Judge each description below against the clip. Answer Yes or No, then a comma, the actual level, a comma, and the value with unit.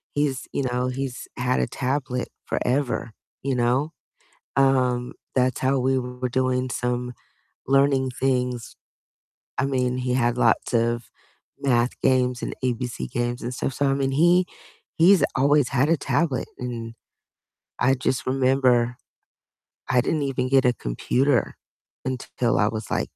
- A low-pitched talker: Yes, low, 130 Hz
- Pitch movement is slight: Yes, narrow, 1.7 semitones